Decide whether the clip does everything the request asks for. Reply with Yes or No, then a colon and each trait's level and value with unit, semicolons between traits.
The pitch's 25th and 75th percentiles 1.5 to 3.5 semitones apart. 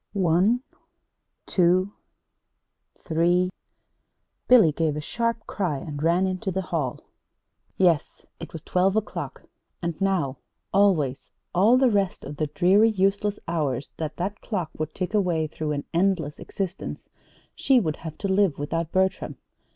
No: average, 3.9 semitones